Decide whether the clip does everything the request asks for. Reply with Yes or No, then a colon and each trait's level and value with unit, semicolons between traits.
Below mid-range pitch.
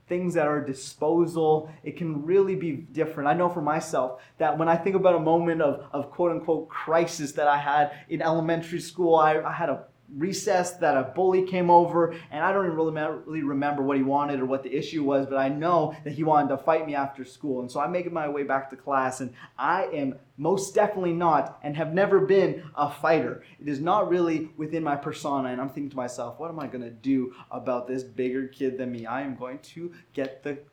No: medium, 155 Hz